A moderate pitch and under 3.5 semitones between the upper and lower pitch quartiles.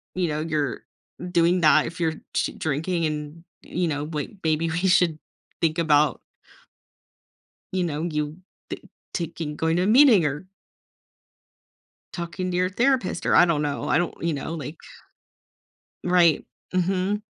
Yes: medium, 165 Hz; average, 2.9 semitones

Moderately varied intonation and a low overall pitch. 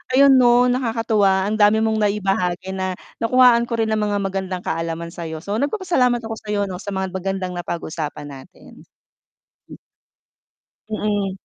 No: average, 3.5 semitones; high, 205 Hz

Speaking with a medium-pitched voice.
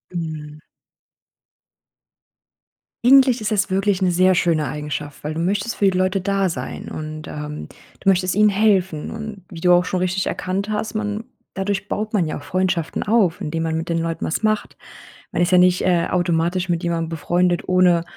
Yes: medium, 180 Hz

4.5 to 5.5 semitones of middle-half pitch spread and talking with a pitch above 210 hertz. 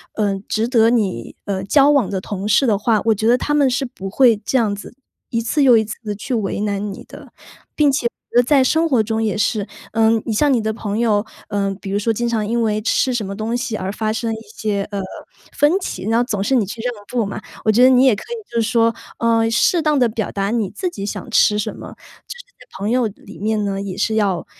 No: average, 3.0 semitones; high, 220 Hz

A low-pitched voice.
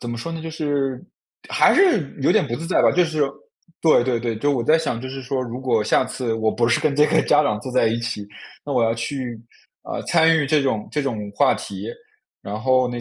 Yes: low, 130 Hz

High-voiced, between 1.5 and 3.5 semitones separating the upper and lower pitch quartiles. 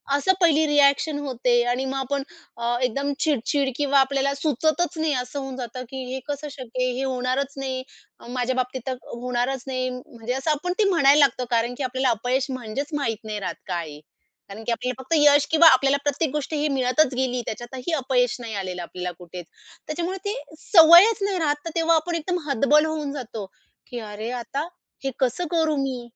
Yes: very high, 270 Hz; average, 3.1 semitones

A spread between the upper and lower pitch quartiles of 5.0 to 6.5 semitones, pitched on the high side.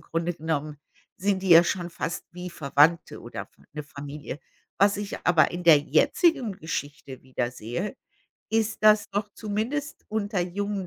No: average, 5.3 semitones; medium, 175 Hz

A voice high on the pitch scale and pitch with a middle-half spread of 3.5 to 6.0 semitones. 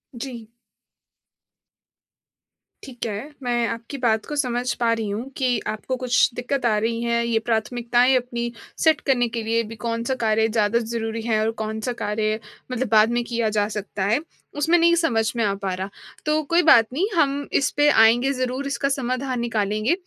No: high, 235 Hz; narrow, 2.6 semitones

